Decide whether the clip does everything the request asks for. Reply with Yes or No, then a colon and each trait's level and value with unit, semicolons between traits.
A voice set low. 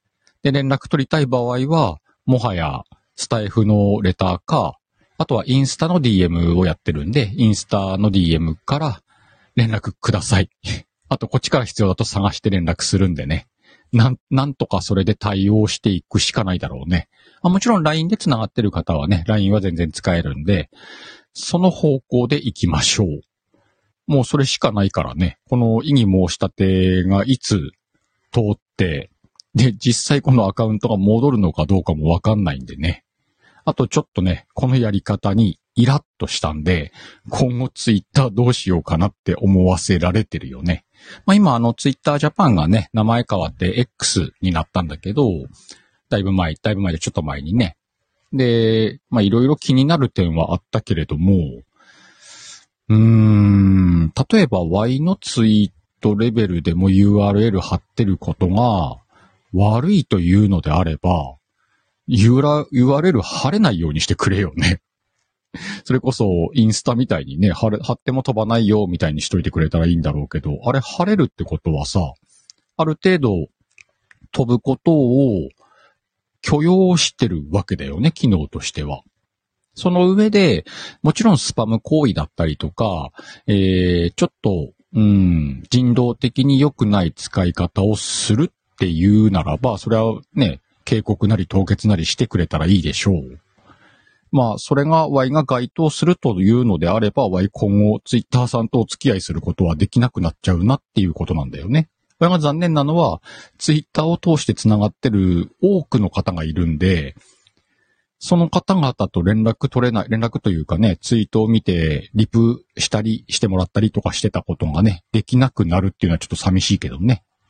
Yes: low, 105 Hz